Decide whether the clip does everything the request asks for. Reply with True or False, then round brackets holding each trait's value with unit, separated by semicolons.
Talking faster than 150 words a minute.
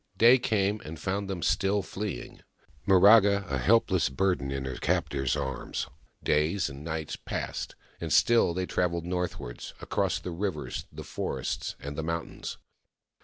False (145 wpm)